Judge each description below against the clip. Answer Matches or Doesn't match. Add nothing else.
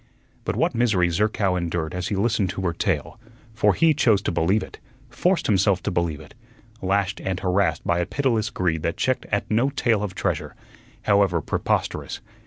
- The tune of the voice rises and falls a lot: Doesn't match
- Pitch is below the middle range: Matches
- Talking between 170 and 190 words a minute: Matches